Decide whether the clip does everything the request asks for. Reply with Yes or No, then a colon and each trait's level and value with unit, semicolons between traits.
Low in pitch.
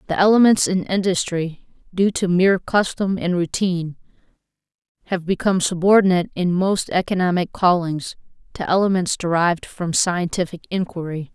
No: medium, 180 Hz